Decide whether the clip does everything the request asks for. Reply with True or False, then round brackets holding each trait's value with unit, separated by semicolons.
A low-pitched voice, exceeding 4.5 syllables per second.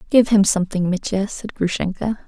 False (200 Hz; 5.5 syllables/s)